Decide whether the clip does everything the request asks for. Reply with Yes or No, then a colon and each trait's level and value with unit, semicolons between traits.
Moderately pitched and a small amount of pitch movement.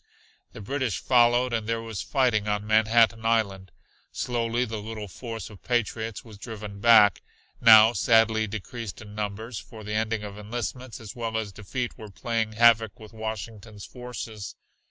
No: low, 110 Hz; narrow, 1.8 semitones